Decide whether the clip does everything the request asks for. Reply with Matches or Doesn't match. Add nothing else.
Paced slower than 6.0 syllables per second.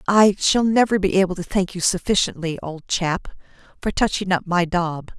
Matches